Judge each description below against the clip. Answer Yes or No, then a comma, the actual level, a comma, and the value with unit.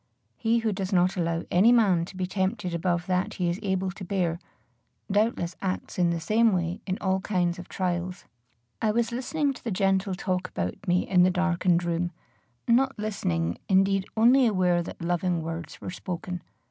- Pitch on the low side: No, medium, 185 Hz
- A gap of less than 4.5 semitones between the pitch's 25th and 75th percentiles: Yes, average, 2.7 semitones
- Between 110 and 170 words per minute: No, average, 185 wpm